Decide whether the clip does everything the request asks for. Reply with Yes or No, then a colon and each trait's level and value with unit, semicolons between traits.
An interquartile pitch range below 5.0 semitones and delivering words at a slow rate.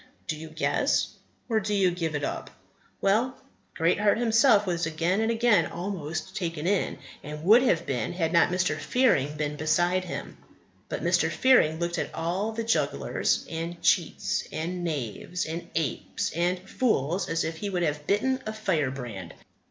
No: average, 4.4 semitones; average, 165 wpm